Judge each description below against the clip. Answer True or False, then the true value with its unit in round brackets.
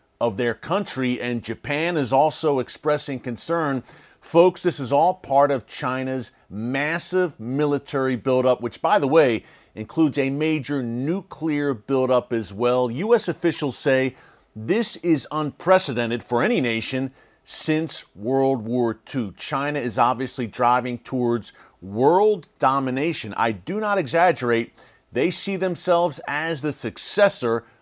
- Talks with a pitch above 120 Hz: True (135 Hz)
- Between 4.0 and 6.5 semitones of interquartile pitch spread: True (5.0 semitones)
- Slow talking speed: True (130 wpm)